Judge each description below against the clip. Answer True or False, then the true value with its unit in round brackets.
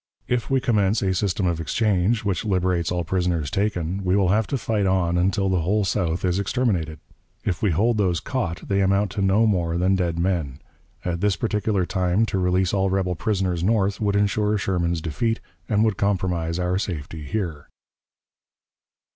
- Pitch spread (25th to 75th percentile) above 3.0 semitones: False (2.7 semitones)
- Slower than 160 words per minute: False (180 wpm)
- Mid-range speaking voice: False (95 Hz)